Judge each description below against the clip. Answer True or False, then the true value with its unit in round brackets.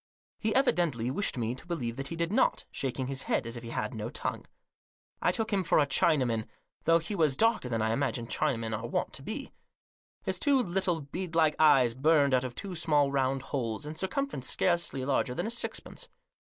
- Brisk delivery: True (210 wpm)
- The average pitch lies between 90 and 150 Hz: True (140 Hz)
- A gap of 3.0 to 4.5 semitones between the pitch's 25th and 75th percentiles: False (5.6 semitones)